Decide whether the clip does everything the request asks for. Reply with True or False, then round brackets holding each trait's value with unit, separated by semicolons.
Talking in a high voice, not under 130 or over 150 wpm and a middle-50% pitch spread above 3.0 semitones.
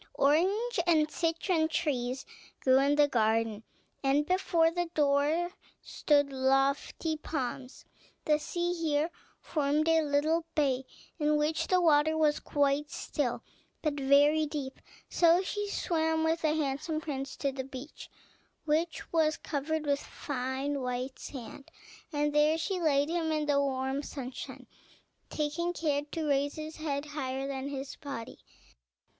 False (295 Hz; 140 wpm; 2.5 semitones)